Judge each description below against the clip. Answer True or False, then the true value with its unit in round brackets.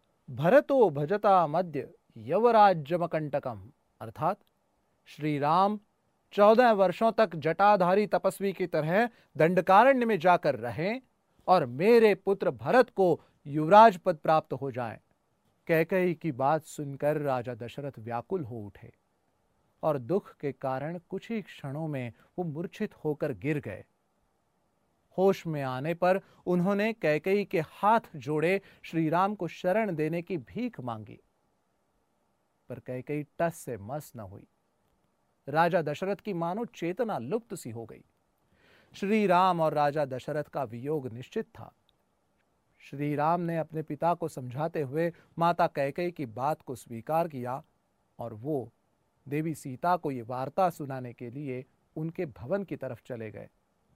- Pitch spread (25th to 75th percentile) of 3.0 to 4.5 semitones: False (5.2 semitones)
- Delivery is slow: False (135 wpm)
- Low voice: False (160 Hz)